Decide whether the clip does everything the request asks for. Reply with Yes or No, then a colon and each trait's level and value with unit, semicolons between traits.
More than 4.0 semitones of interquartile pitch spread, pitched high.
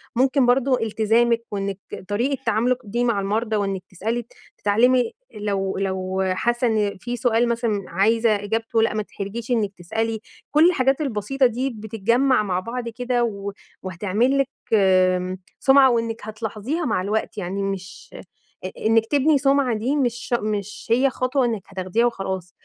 No: average, 3.6 semitones; high, 225 Hz